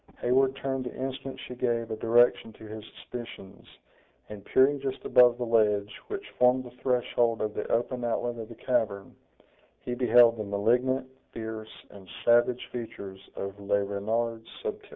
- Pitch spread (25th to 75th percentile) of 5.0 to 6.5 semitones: No, narrow, 2.5 semitones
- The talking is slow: No, average, 160 wpm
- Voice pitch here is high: No, low, 120 Hz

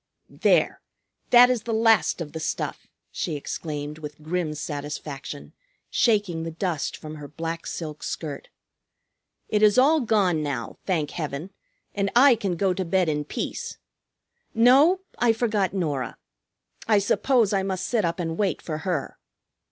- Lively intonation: Yes, wide, 5.8 semitones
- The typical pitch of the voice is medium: Yes, medium, 180 Hz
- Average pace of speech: Yes, average, 150 wpm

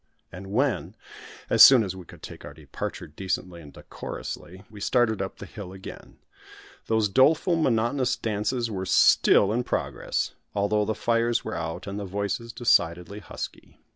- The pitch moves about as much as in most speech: Yes, average, 3.7 semitones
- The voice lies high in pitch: No, low, 105 Hz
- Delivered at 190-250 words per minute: No, average, 160 wpm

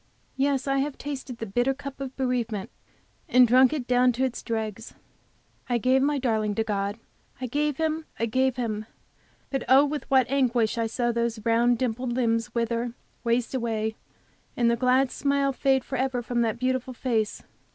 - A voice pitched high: Yes, very high, 250 Hz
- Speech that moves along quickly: No, average, 175 wpm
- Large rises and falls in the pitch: No, narrow, 2.5 semitones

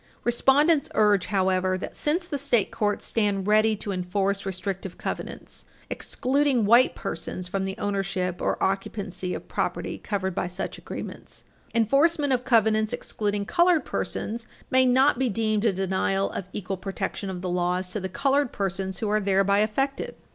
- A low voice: No, high, 205 Hz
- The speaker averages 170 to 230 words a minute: No, average, 160 wpm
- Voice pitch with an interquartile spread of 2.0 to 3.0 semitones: No, average, 4.1 semitones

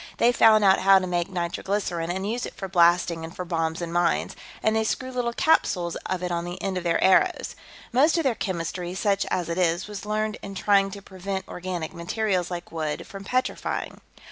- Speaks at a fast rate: Yes, fast, 210 wpm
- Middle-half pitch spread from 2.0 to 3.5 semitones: Yes, average, 3.2 semitones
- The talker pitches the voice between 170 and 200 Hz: Yes, medium, 185 Hz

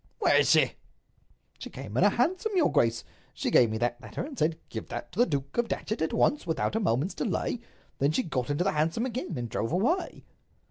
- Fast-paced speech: Yes, fast, 220 wpm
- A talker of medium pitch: Yes, medium, 170 Hz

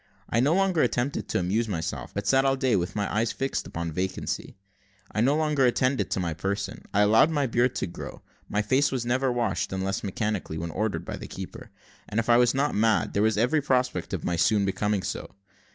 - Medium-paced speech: No, fast, 215 wpm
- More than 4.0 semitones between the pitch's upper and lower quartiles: Yes, average, 4.8 semitones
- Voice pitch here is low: Yes, low, 115 Hz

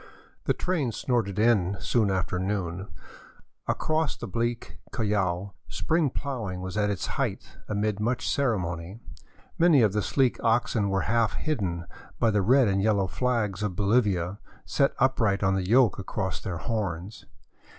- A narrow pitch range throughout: No, average, 3.9 semitones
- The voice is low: Yes, low, 105 Hz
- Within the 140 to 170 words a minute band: Yes, average, 150 wpm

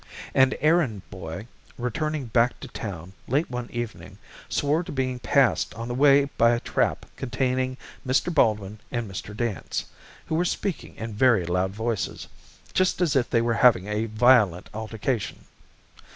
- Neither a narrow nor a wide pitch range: Yes, average, 3.7 semitones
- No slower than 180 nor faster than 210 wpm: No, average, 155 wpm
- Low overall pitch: Yes, low, 120 Hz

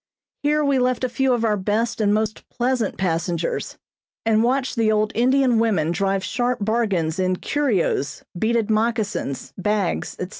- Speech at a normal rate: Yes, average, 155 wpm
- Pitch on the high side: Yes, high, 220 Hz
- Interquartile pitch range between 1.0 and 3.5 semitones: No, average, 4.0 semitones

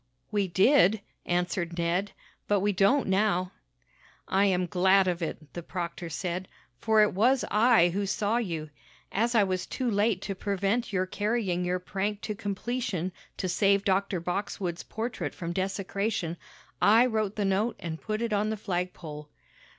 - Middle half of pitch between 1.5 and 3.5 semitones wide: Yes, average, 3.0 semitones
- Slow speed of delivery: No, average, 160 wpm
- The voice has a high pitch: Yes, high, 195 Hz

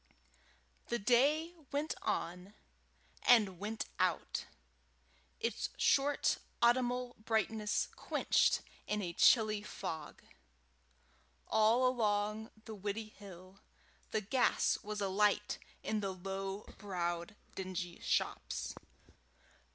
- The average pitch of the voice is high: Yes, high, 210 Hz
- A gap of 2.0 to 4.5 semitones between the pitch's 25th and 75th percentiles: Yes, average, 3.5 semitones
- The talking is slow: Yes, slow, 90 wpm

